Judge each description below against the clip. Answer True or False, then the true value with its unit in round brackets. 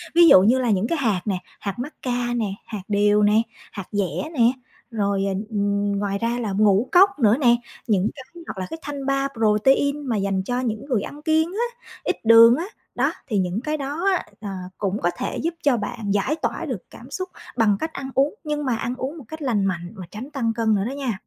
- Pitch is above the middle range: True (230 Hz)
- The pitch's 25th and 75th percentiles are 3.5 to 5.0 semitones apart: False (5.5 semitones)